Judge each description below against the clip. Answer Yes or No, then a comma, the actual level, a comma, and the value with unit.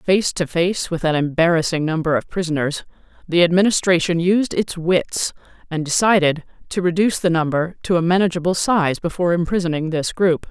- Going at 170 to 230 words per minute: No, average, 160 wpm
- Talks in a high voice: No, medium, 170 Hz